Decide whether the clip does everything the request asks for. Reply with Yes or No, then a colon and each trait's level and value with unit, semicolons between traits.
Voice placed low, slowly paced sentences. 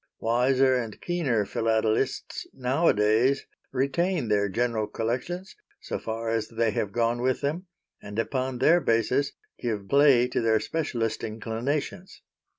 Yes: low, 120 Hz; slow, 130 wpm